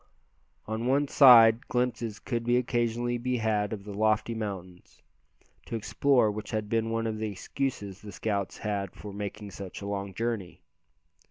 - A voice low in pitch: Yes, low, 110 Hz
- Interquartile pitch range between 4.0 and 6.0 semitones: No, narrow, 2.6 semitones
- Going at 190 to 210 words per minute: No, average, 160 wpm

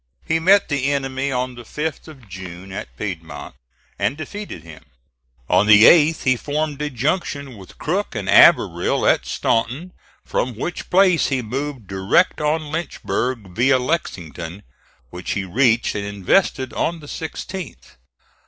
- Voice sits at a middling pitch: No, low, 130 Hz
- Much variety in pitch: Yes, wide, 7.3 semitones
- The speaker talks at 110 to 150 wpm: Yes, average, 145 wpm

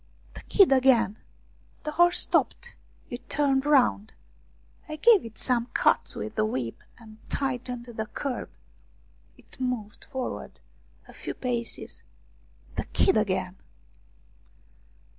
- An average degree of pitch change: Yes, average, 4.0 semitones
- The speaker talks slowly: Yes, slow, 120 wpm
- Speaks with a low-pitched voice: No, very high, 250 Hz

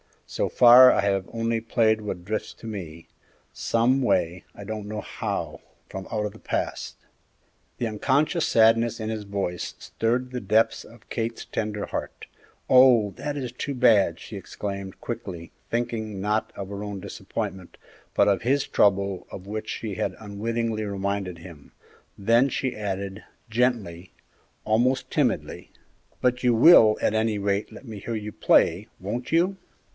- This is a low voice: Yes, low, 110 Hz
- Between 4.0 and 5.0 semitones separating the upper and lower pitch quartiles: No, average, 3.0 semitones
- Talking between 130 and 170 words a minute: Yes, average, 155 wpm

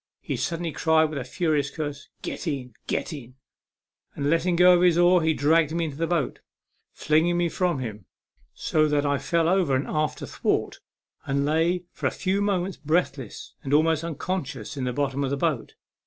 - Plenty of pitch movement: No, average, 3.5 semitones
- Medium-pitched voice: Yes, medium, 155 Hz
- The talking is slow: No, average, 195 wpm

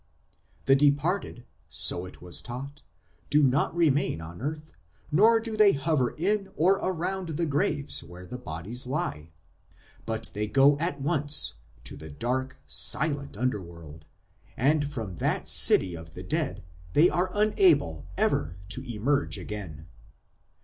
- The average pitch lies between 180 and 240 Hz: No, low, 135 Hz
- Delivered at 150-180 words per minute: No, average, 140 wpm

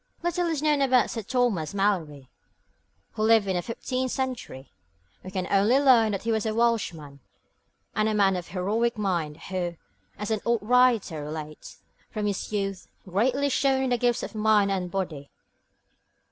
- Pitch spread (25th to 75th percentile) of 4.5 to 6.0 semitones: Yes, average, 5.0 semitones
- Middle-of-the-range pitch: No, high, 215 Hz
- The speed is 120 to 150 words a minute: No, average, 160 wpm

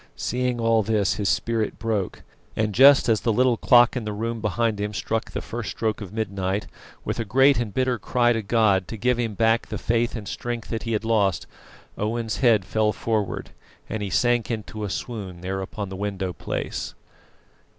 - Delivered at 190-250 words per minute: Yes, average, 195 wpm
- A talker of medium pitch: No, low, 110 Hz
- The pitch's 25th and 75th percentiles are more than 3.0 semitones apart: No, narrow, 2.4 semitones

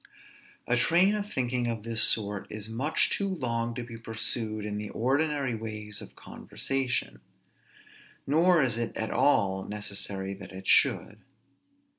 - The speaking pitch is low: Yes, low, 115 Hz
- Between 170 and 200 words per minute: No, average, 145 wpm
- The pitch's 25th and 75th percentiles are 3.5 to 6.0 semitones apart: Yes, average, 4.3 semitones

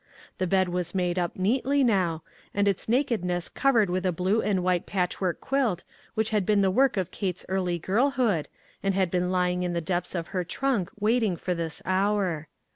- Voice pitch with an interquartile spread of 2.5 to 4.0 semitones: Yes, average, 3.0 semitones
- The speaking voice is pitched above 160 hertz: Yes, medium, 185 Hz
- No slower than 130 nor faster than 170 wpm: No, average, 200 wpm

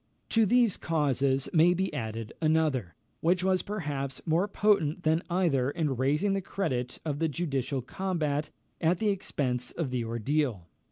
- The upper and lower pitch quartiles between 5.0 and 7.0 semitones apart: Yes, average, 5.3 semitones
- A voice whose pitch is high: No, medium, 155 Hz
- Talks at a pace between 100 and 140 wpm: No, average, 155 wpm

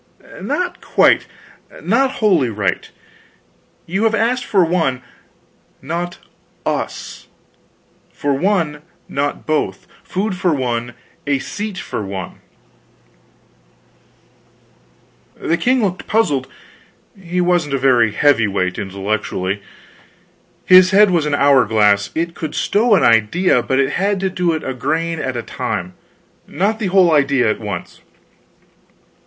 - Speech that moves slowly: Yes, slow, 125 wpm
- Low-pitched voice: No, medium, 155 Hz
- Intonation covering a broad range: Yes, wide, 7.5 semitones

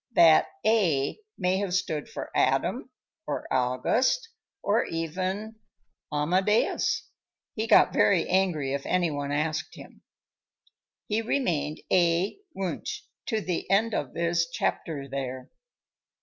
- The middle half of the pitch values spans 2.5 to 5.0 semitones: No, wide, 5.4 semitones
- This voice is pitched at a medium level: Yes, medium, 175 Hz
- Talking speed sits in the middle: No, slow, 120 wpm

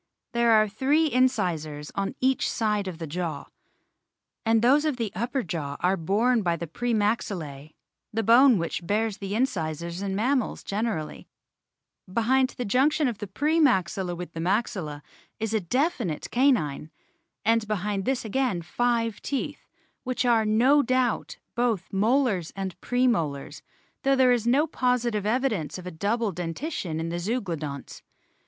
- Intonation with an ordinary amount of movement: No, wide, 5.9 semitones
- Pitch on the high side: Yes, high, 215 Hz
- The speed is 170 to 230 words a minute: No, average, 155 wpm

